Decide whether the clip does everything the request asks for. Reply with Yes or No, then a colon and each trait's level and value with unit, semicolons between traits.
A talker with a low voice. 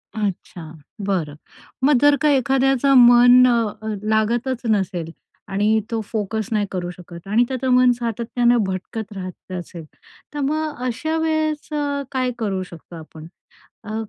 No: high, 230 Hz